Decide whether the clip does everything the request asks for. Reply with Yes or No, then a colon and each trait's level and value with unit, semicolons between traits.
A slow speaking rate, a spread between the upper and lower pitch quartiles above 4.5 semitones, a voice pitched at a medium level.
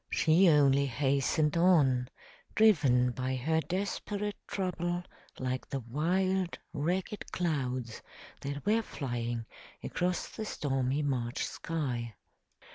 Yes: slow, 105 wpm; wide, 5.6 semitones; medium, 145 Hz